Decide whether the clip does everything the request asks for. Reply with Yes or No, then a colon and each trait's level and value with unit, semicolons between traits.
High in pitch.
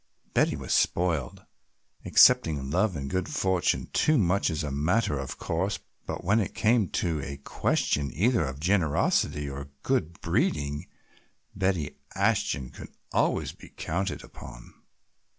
No: very low, 80 Hz